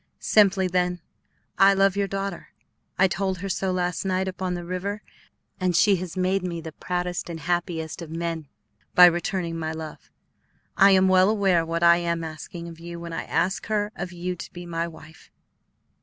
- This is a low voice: No, medium, 180 Hz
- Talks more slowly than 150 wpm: No, average, 185 wpm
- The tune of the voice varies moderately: No, narrow, 2.0 semitones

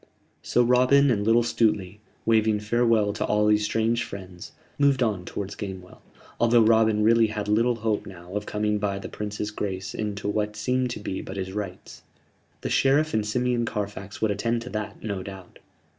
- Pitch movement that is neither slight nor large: No, narrow, 2.3 semitones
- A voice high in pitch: No, low, 105 Hz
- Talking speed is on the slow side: No, average, 180 wpm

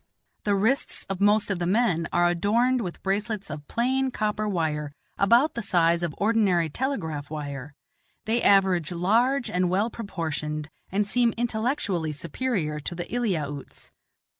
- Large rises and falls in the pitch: Yes, wide, 5.8 semitones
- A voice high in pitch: Yes, high, 195 Hz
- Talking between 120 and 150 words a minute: Yes, average, 145 wpm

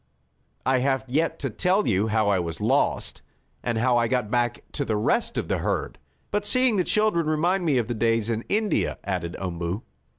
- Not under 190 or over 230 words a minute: Yes, average, 200 wpm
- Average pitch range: No, wide, 7.8 semitones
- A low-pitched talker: Yes, low, 120 Hz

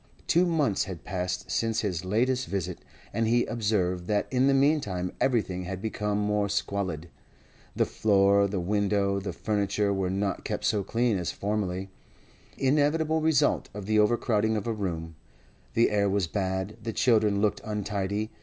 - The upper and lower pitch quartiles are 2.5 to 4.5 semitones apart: Yes, average, 2.8 semitones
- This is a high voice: No, low, 105 Hz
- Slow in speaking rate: No, average, 155 wpm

